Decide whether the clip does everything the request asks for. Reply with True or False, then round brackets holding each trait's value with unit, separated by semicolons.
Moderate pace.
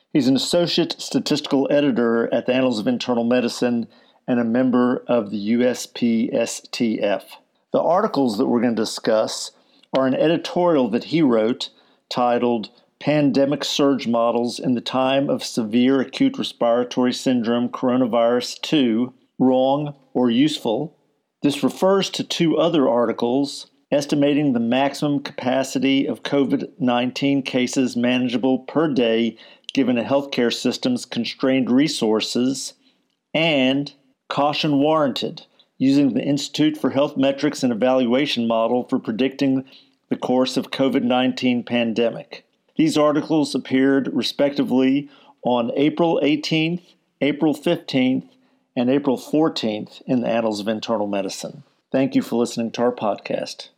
False (125 wpm)